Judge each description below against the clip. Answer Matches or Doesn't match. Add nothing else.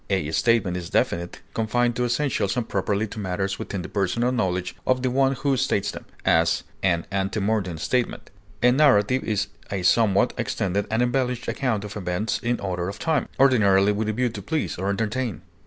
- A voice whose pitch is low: Matches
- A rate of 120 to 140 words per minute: Doesn't match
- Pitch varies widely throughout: Doesn't match